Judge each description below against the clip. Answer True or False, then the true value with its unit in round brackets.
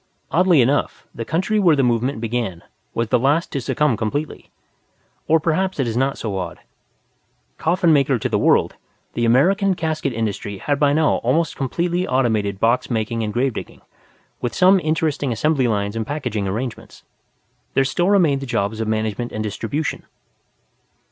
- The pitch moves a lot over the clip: True (5.9 semitones)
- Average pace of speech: True (160 wpm)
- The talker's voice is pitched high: False (130 Hz)